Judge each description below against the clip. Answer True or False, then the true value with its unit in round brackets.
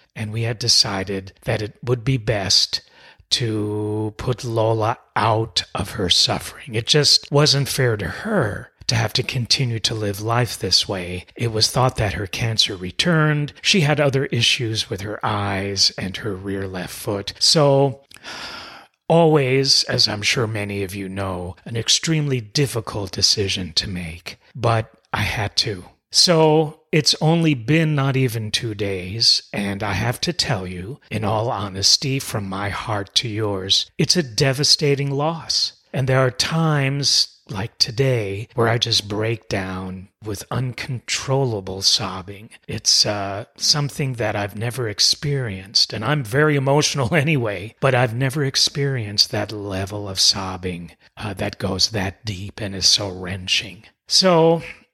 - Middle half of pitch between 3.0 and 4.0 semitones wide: False (5.2 semitones)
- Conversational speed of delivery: True (150 wpm)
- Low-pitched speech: True (110 Hz)